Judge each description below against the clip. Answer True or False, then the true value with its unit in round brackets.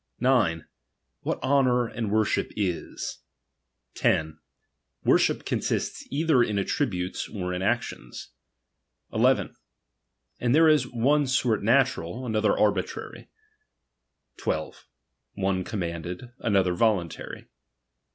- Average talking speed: False (100 wpm)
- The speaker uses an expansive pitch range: True (5.7 semitones)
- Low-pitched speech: True (110 Hz)